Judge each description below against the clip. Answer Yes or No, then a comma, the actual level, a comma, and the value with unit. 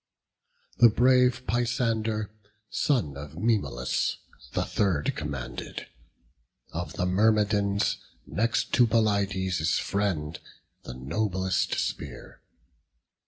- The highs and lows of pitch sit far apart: Yes, wide, 5.9 semitones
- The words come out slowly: Yes, slow, 85 wpm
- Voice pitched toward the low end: Yes, low, 100 Hz